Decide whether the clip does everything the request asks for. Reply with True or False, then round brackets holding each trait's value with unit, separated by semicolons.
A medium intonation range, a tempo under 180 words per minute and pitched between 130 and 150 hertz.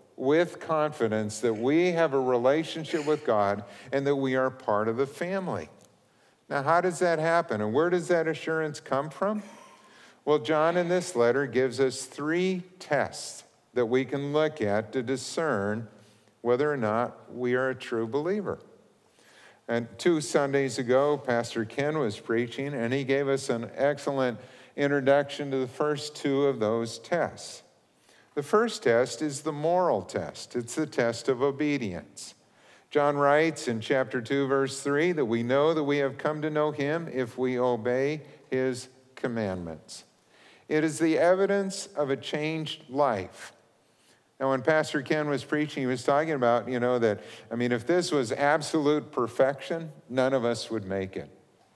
True (3.8 semitones; 165 wpm; 140 Hz)